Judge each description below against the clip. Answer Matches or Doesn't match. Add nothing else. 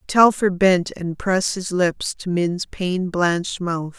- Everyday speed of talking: Matches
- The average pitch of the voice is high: Doesn't match